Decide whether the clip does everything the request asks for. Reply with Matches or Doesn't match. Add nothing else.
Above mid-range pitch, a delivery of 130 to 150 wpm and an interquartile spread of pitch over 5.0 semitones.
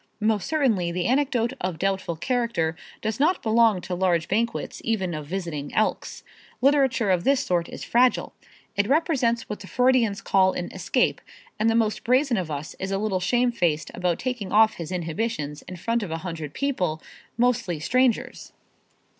Doesn't match